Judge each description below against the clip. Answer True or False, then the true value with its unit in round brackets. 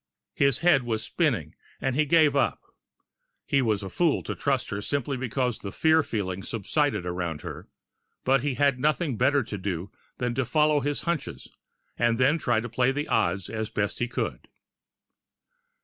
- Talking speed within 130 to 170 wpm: False (180 wpm)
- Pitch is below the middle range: True (125 Hz)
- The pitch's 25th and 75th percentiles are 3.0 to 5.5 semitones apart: True (5.1 semitones)